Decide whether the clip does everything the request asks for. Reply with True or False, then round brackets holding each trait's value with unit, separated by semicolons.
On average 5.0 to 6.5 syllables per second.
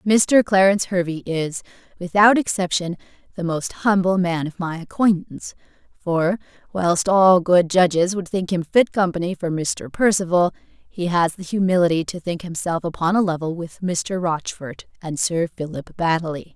False (4.7 syllables/s)